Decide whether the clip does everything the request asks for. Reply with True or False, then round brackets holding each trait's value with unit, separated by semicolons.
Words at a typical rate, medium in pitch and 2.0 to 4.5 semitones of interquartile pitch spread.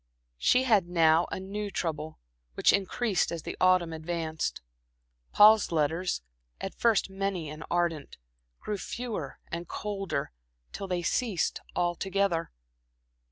False (120 wpm; 180 Hz; 3.5 semitones)